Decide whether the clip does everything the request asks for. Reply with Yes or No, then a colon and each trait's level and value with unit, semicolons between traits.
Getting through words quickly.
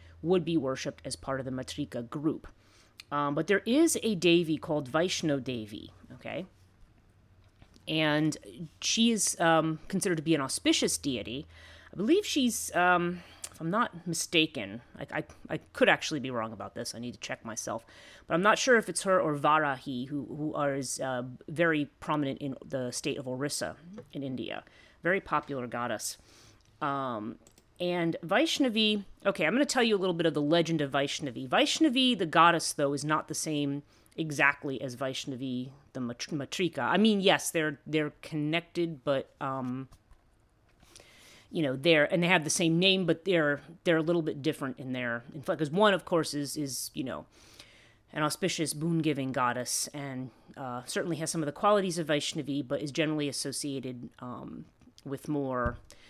No: average, 175 wpm